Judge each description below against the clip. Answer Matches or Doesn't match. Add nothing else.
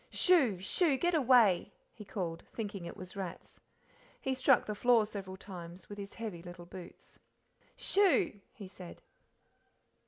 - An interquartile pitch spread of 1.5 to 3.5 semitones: Doesn't match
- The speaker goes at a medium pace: Matches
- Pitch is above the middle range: Matches